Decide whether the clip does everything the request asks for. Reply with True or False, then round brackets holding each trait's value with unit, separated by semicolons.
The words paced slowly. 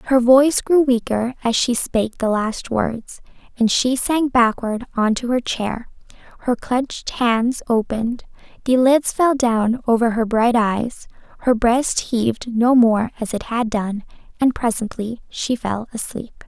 False (160 wpm)